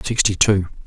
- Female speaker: No, male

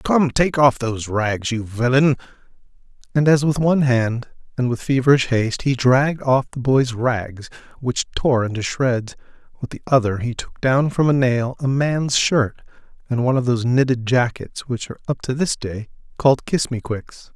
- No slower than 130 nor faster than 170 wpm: No, average, 185 wpm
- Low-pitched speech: Yes, low, 130 Hz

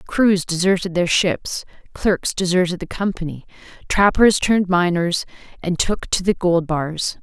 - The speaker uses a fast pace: No, average, 140 wpm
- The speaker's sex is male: No, female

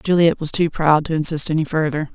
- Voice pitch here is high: No, medium, 155 Hz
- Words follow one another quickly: Yes, fast, 225 wpm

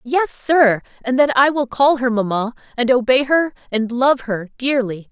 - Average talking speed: Yes, average, 190 wpm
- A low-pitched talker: No, very high, 250 Hz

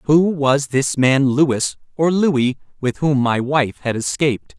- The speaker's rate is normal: Yes, average, 145 wpm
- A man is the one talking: Yes, male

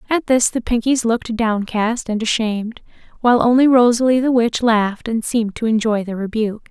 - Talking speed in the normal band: Yes, average, 180 wpm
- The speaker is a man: No, female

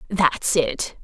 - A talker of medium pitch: Yes, medium, 180 Hz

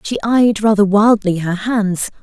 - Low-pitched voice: No, high, 210 Hz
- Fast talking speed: No, average, 160 wpm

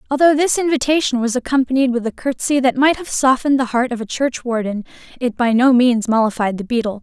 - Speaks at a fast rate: Yes, fast, 215 wpm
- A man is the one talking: No, female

